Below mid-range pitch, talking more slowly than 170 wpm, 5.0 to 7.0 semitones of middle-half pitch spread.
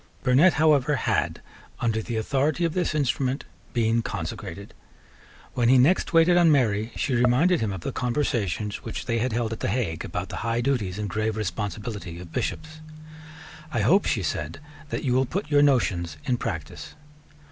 No: low, 120 Hz; average, 175 wpm; average, 5.3 semitones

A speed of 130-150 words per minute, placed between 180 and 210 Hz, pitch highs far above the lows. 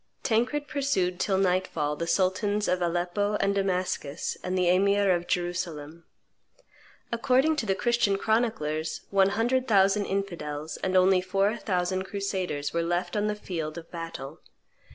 No: average, 145 wpm; high, 190 Hz; average, 2.9 semitones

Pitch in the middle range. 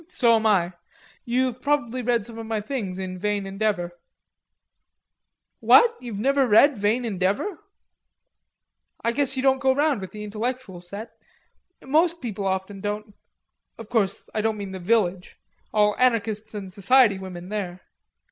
No: high, 215 Hz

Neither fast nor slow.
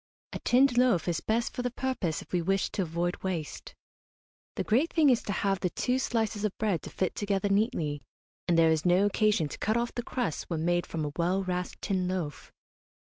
No: fast, 215 wpm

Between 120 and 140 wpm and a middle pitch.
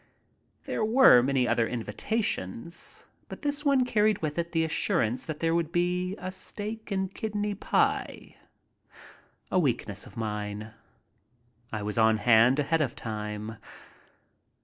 Yes: slow, 135 wpm; medium, 160 Hz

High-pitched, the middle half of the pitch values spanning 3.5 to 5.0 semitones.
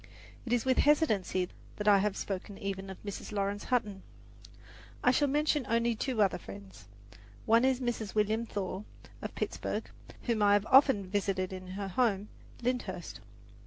Yes: high, 205 Hz; average, 3.9 semitones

